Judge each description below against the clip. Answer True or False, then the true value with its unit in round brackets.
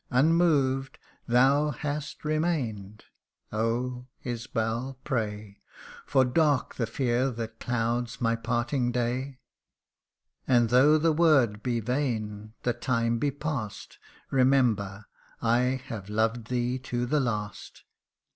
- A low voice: True (125 Hz)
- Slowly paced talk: True (110 wpm)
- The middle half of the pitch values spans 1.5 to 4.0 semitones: True (2.9 semitones)